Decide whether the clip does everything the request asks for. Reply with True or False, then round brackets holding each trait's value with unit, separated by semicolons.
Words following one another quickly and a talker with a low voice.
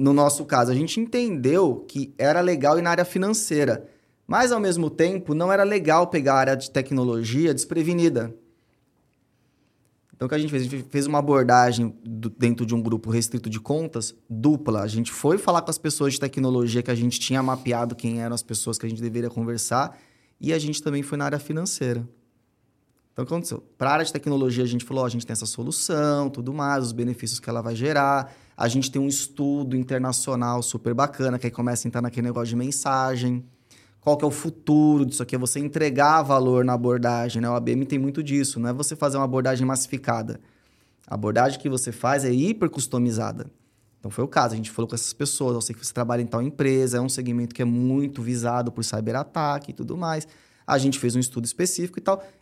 True (220 wpm; 130 Hz)